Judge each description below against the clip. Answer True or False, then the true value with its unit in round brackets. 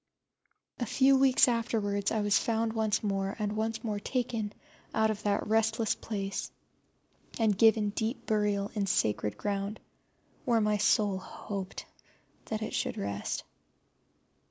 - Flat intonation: True (1.8 semitones)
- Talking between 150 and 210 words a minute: False (135 wpm)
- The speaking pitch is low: False (215 Hz)